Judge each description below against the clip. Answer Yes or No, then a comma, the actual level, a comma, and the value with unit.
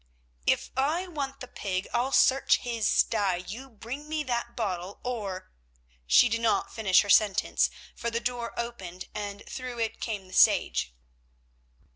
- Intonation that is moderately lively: Yes, average, 3.9 semitones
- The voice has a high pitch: Yes, high, 230 Hz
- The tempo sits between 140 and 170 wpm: Yes, average, 150 wpm